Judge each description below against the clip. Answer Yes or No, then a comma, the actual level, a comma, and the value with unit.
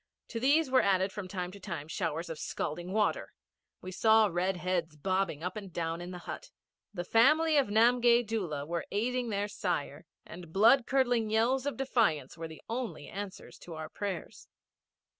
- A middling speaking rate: Yes, average, 180 wpm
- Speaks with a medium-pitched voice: No, high, 200 Hz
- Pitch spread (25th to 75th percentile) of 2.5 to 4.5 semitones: No, average, 5.1 semitones